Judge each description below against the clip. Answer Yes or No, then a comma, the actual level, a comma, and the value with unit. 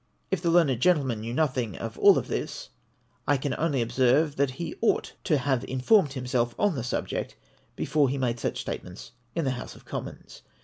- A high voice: No, low, 135 Hz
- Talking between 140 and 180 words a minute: No, average, 190 wpm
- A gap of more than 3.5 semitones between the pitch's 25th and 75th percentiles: Yes, average, 3.9 semitones